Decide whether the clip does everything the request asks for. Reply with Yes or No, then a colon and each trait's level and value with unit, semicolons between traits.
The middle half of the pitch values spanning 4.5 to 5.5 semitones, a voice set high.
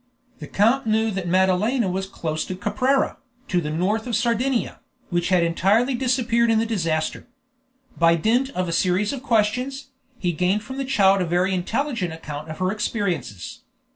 Yes: average, 5.0 semitones; high, 200 Hz